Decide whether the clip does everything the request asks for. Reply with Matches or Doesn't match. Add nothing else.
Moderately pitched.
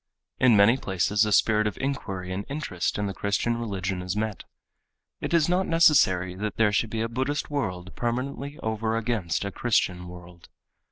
Doesn't match